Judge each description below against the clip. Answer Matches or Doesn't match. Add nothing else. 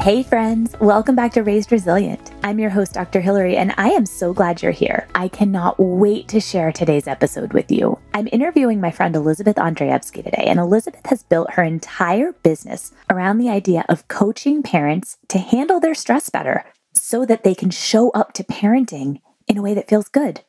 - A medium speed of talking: Matches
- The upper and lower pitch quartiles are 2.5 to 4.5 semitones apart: Matches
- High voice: Matches